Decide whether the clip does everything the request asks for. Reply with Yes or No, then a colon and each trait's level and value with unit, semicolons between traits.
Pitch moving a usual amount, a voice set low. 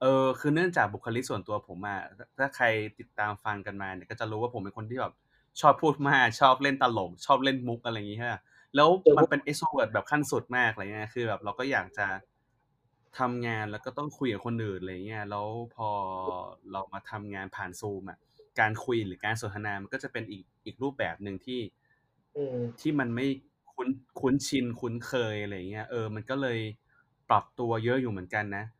Yes: average, 3.9 semitones; low, 115 Hz